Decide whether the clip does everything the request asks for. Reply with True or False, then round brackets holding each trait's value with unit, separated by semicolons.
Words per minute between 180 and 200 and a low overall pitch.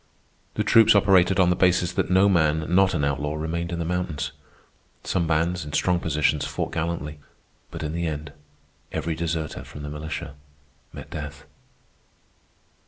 False (160 wpm; 80 Hz)